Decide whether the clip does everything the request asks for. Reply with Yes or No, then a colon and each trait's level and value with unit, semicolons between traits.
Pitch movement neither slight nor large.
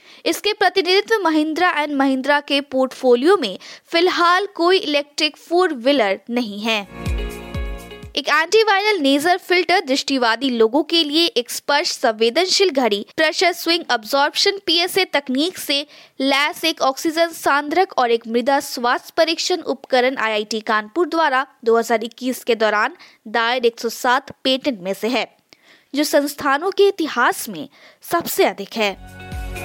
No: wide, 6.0 semitones